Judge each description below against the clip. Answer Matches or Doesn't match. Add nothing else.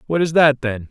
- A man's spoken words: Matches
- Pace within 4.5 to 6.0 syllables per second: Matches